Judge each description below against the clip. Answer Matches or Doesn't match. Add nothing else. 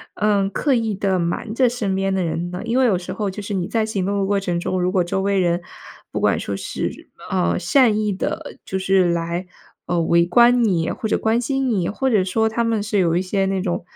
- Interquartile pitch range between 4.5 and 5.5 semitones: Doesn't match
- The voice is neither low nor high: Doesn't match